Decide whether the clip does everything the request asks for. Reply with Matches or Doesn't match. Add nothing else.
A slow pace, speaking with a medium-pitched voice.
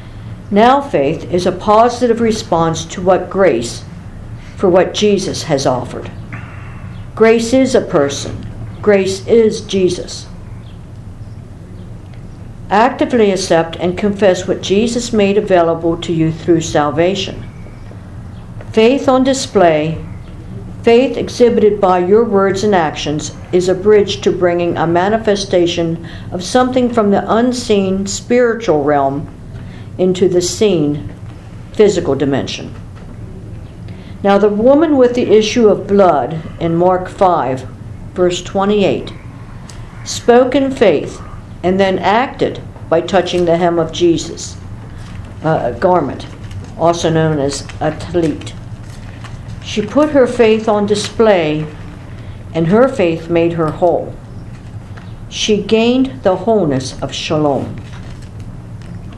Matches